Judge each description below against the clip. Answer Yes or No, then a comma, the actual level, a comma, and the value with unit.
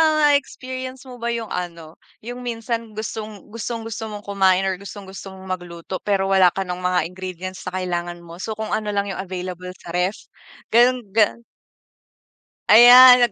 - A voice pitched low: No, high, 200 Hz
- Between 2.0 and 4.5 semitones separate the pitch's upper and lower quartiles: Yes, average, 4.1 semitones